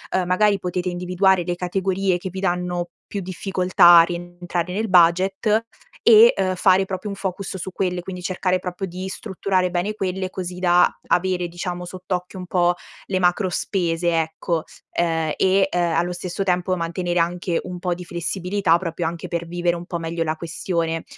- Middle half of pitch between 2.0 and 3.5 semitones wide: No, narrow, 1.4 semitones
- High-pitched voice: No, medium, 180 Hz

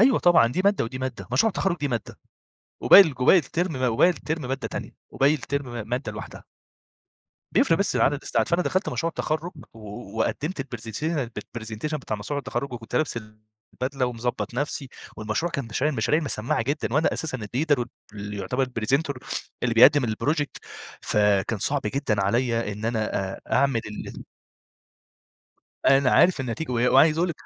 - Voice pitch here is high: No, low, 130 Hz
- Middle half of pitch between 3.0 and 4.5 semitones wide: No, average, 5.0 semitones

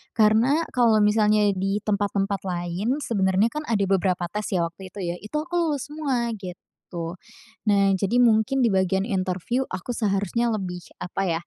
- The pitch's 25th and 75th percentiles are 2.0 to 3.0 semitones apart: No, average, 3.8 semitones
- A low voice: No, high, 205 Hz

